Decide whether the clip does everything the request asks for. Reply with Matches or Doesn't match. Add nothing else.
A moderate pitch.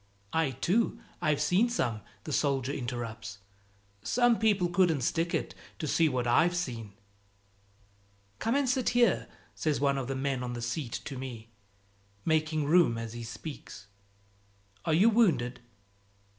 Matches